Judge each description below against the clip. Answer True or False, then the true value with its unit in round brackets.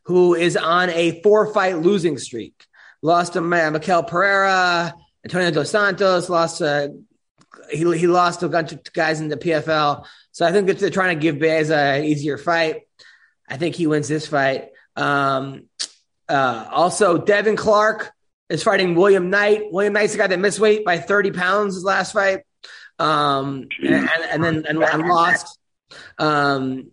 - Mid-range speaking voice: True (170 Hz)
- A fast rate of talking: False (170 wpm)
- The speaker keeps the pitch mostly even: False (3.9 semitones)